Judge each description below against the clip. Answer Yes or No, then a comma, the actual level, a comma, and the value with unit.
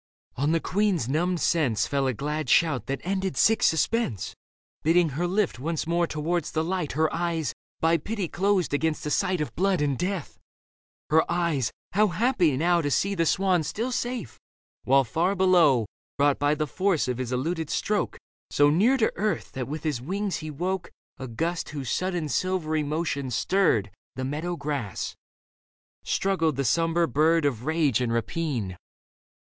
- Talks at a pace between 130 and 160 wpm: No, average, 170 wpm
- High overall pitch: No, medium, 160 Hz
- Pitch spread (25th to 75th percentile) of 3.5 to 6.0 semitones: Yes, average, 4.2 semitones